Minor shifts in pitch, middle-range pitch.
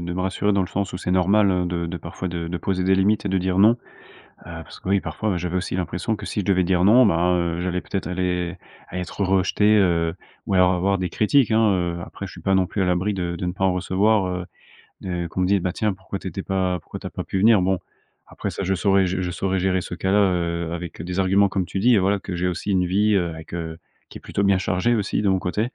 No: narrow, 1.8 semitones; very low, 95 Hz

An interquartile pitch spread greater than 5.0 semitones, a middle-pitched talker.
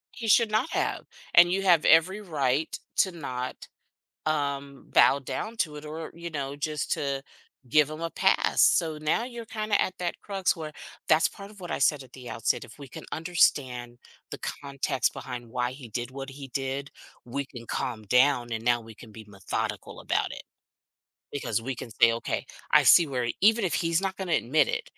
Yes: wide, 5.5 semitones; medium, 145 Hz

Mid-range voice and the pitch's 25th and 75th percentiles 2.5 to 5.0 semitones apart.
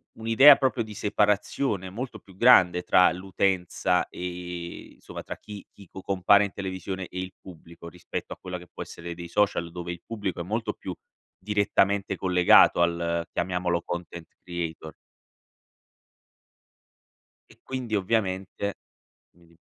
No: very low, 95 Hz; average, 2.8 semitones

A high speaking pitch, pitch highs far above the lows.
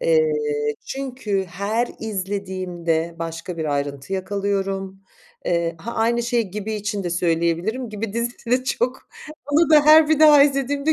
Yes: high, 205 Hz; wide, 6.1 semitones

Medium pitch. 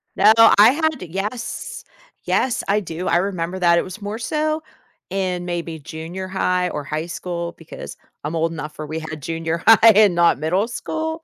Yes: medium, 180 Hz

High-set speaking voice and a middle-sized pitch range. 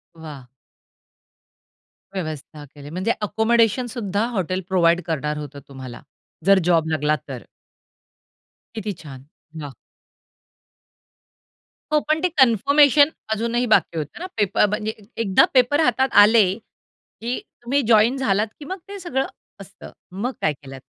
No: high, 205 Hz; wide, 7.7 semitones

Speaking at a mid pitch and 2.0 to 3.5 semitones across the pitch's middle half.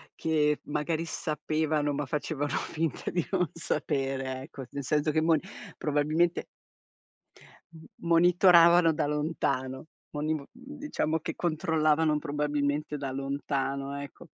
Yes: medium, 150 Hz; narrow, 2.3 semitones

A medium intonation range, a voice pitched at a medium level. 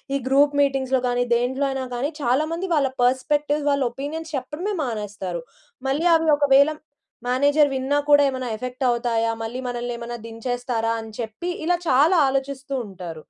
No: average, 3.2 semitones; very high, 265 Hz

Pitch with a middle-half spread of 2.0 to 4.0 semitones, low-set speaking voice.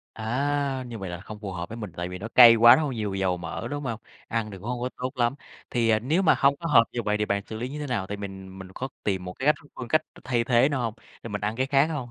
No: average, 4.5 semitones; low, 115 Hz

